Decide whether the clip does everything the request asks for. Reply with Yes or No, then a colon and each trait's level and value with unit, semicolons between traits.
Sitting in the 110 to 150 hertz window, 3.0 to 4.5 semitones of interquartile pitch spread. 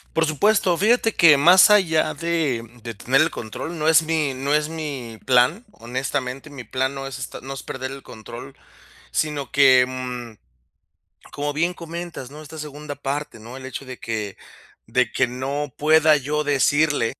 Yes: medium, 140 Hz; average, 3.6 semitones